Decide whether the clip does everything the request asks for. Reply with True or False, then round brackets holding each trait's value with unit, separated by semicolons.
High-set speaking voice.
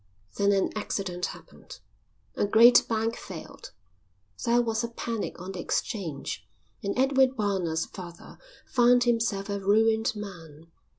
True (210 Hz)